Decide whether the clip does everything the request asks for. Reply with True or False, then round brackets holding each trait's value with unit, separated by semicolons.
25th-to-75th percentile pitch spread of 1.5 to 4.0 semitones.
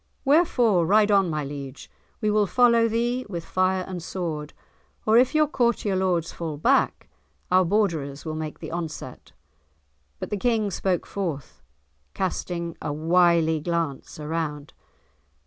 False (5.1 semitones)